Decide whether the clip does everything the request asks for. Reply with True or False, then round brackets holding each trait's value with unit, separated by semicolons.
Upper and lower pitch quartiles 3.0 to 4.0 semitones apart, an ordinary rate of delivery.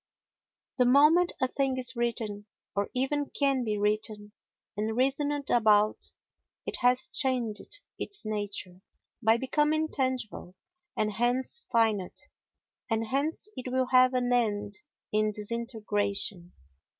False (3.7 semitones; 120 wpm)